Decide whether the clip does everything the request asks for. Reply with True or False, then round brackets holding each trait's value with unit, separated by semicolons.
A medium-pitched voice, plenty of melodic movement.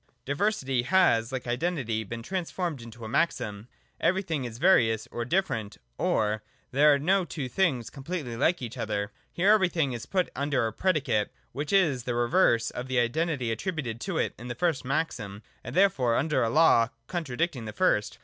False (130 Hz; 6.5 semitones)